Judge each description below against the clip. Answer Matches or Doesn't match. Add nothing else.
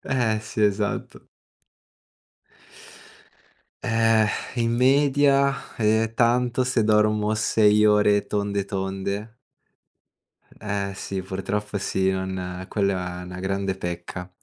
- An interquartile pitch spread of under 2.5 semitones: Doesn't match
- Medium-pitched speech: Doesn't match